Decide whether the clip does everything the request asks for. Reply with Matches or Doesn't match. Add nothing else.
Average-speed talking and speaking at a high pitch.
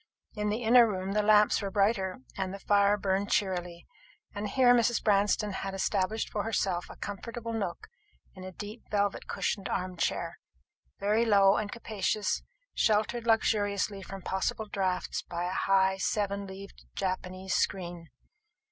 Matches